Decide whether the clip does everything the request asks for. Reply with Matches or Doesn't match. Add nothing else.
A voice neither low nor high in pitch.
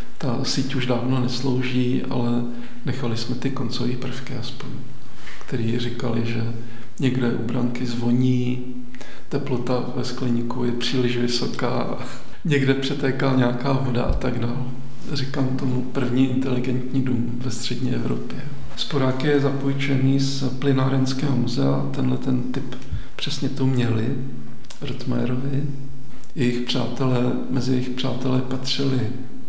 Doesn't match